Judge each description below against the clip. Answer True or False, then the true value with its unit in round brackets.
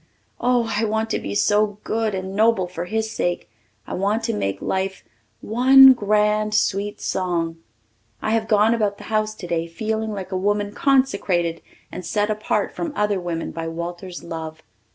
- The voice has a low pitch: False (205 Hz)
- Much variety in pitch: False (3.4 semitones)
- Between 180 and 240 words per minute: False (170 wpm)